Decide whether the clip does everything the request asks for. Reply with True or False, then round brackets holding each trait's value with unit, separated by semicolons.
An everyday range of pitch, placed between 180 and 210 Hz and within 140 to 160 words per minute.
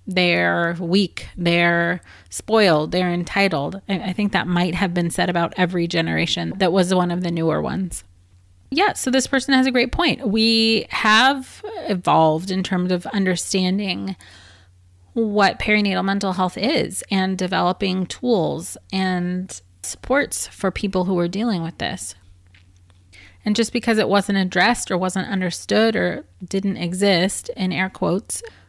True (3.0 semitones; 185 Hz; 145 wpm)